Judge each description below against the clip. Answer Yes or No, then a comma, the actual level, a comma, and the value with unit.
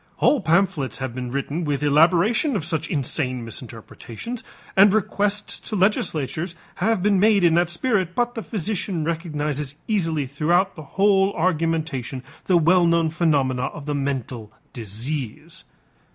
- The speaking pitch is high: No, medium, 165 Hz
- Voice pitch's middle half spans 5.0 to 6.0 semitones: Yes, wide, 5.5 semitones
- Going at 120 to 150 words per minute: Yes, average, 140 wpm